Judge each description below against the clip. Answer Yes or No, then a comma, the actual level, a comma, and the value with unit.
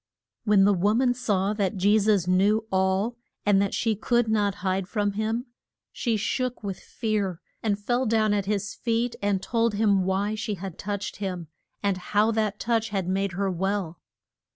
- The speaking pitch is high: Yes, high, 205 Hz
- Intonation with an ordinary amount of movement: No, narrow, 2.2 semitones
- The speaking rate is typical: Yes, average, 180 wpm